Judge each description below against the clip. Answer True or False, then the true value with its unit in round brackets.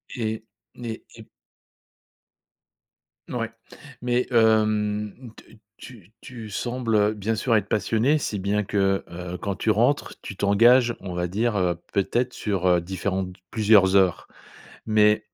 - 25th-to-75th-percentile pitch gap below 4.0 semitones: True (2.7 semitones)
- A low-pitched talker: True (105 Hz)